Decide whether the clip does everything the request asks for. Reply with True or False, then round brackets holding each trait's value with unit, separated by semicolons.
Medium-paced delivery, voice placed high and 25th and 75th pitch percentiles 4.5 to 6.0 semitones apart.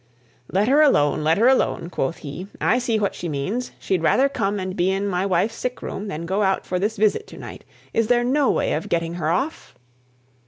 False (225 wpm; 195 Hz; 5.4 semitones)